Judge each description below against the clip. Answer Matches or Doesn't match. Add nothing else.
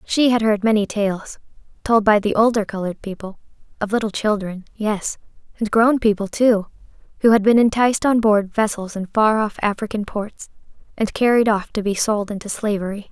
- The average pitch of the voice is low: Doesn't match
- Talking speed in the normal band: Matches